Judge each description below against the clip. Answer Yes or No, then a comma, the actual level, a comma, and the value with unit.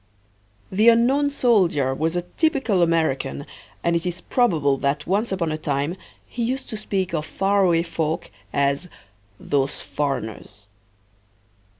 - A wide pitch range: Yes, wide, 6.3 semitones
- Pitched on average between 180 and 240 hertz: No, medium, 170 Hz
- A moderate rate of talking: No, slow, 130 wpm